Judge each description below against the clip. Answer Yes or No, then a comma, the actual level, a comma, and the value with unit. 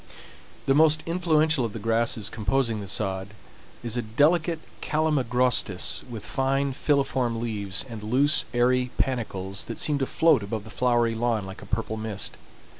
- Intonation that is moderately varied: Yes, average, 4.0 semitones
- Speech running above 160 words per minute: No, average, 155 wpm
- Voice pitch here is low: Yes, low, 120 Hz